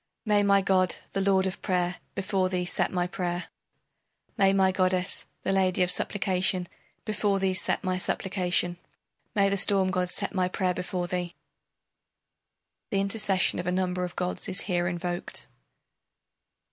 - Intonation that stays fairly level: Yes, narrow, 1.4 semitones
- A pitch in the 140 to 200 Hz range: Yes, medium, 185 Hz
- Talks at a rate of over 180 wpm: No, average, 155 wpm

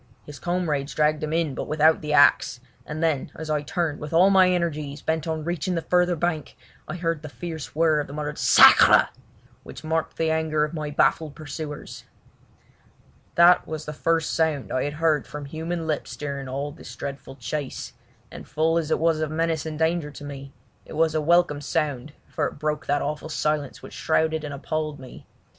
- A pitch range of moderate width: No, narrow, 1.8 semitones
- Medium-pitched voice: Yes, medium, 155 Hz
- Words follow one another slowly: No, average, 195 wpm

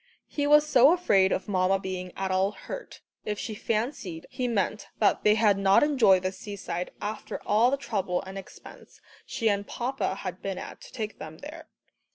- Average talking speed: Yes, average, 190 wpm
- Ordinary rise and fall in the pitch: Yes, average, 4.0 semitones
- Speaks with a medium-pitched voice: No, high, 205 Hz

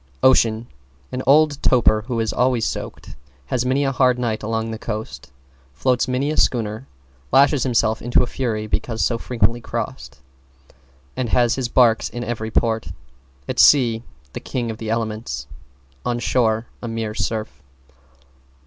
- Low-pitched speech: Yes, low, 115 Hz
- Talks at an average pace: Yes, average, 155 wpm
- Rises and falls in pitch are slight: Yes, narrow, 2.3 semitones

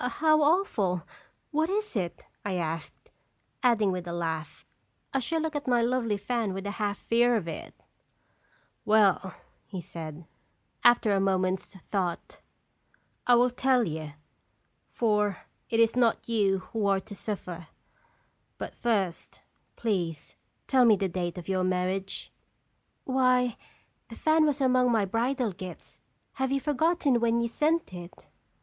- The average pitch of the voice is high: Yes, high, 215 Hz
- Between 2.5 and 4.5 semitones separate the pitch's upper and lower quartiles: No, average, 5.3 semitones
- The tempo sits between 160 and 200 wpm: No, average, 150 wpm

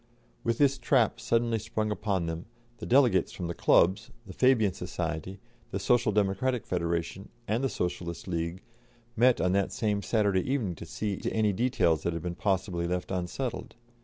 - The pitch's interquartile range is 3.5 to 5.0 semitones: Yes, average, 4.7 semitones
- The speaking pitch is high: No, low, 100 Hz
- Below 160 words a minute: No, average, 170 wpm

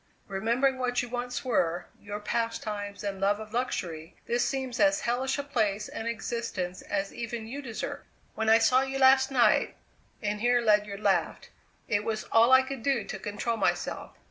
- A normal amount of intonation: Yes, average, 3.5 semitones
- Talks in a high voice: Yes, high, 230 Hz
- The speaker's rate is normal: Yes, average, 175 wpm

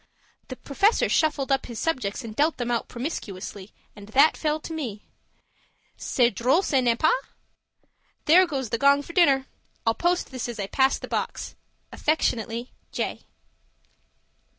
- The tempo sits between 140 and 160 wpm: Yes, average, 150 wpm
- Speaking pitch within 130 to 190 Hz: No, very high, 265 Hz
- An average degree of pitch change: Yes, average, 4.9 semitones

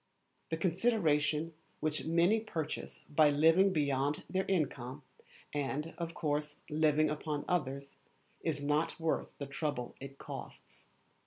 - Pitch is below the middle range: No, medium, 150 Hz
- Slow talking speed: Yes, slow, 125 wpm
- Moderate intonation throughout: No, narrow, 2.3 semitones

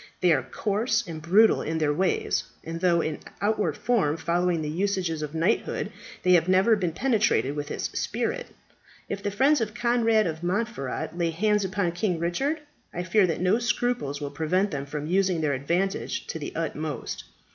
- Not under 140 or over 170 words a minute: No, average, 180 wpm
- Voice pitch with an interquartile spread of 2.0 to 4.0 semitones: No, average, 4.7 semitones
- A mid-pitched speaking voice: Yes, medium, 180 Hz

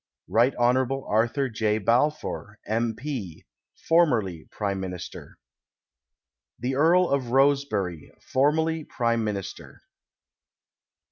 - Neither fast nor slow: No, slow, 95 wpm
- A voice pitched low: Yes, low, 120 Hz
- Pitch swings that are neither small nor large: Yes, average, 4.9 semitones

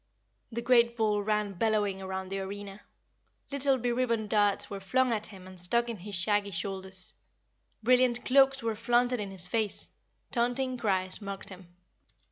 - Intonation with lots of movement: No, average, 3.7 semitones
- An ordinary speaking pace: Yes, average, 155 wpm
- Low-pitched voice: No, high, 210 Hz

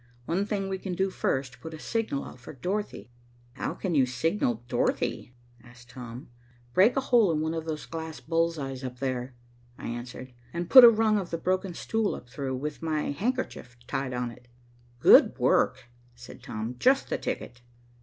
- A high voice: No, medium, 150 Hz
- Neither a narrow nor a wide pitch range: No, wide, 7.2 semitones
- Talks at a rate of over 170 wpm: Yes, average, 185 wpm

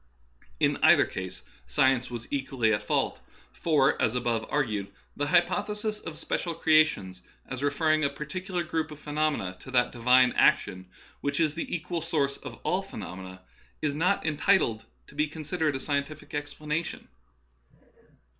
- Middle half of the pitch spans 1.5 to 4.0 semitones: No, average, 4.7 semitones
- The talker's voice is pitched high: No, medium, 145 Hz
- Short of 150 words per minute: No, average, 155 wpm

